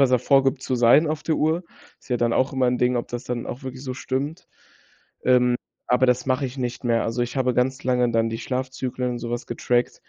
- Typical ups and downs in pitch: No, narrow, 1.5 semitones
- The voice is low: Yes, low, 125 Hz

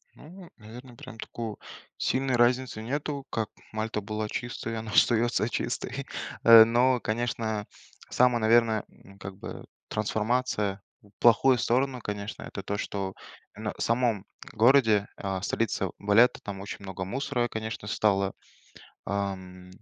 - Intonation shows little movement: No, average, 3.0 semitones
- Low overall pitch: Yes, low, 110 Hz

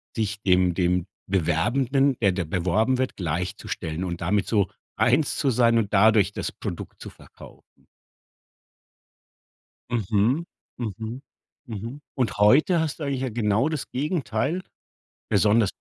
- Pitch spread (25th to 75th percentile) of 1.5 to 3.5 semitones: No, average, 5.2 semitones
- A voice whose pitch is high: No, low, 110 Hz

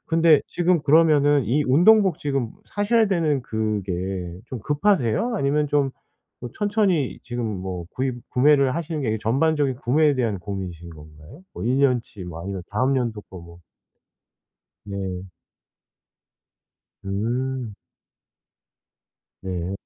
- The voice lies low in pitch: Yes, low, 130 Hz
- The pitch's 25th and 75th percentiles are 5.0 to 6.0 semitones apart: No, wide, 7.3 semitones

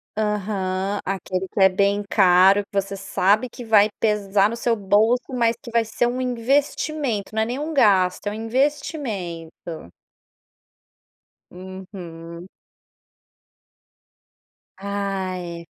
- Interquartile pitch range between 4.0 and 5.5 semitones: No, average, 3.6 semitones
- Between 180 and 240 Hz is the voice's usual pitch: Yes, high, 200 Hz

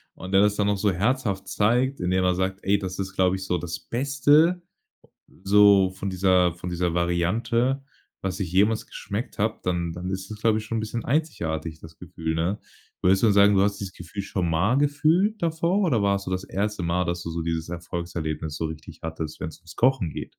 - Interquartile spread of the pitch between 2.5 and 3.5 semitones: No, average, 4.1 semitones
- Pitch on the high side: No, very low, 95 Hz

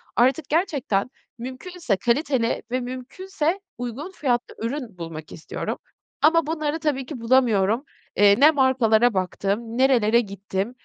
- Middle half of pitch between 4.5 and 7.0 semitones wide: Yes, average, 5.1 semitones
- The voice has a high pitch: Yes, very high, 250 Hz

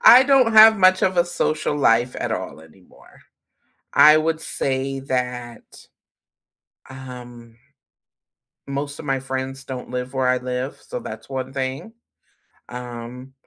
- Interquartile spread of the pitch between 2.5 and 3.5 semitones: Yes, average, 2.9 semitones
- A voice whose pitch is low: Yes, low, 130 Hz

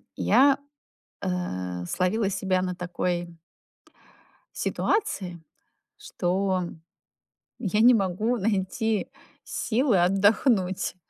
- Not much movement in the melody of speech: No, average, 3.5 semitones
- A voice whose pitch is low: No, high, 190 Hz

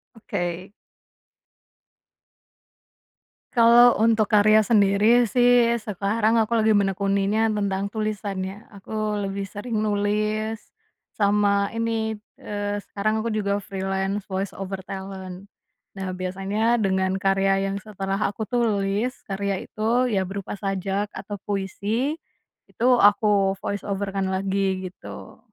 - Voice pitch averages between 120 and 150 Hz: No, high, 205 Hz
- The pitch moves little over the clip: Yes, narrow, 2.0 semitones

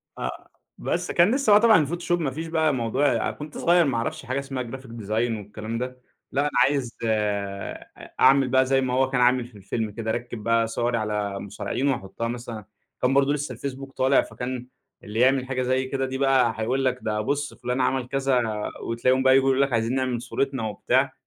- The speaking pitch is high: No, low, 130 Hz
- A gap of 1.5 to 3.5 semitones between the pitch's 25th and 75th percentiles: Yes, average, 2.9 semitones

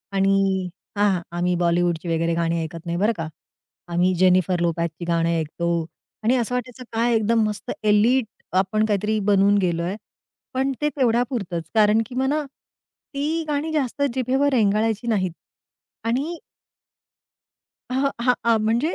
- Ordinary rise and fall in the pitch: No, wide, 6.0 semitones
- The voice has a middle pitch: No, high, 210 Hz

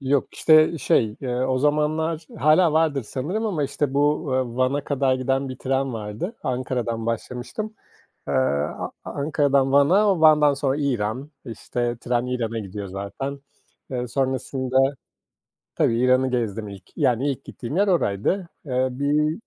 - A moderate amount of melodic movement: Yes, average, 3.5 semitones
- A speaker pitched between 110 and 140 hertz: Yes, low, 135 Hz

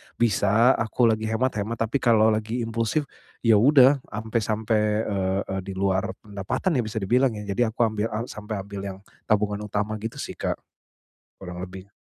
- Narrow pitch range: Yes, narrow, 2.3 semitones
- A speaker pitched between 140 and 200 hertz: No, low, 110 Hz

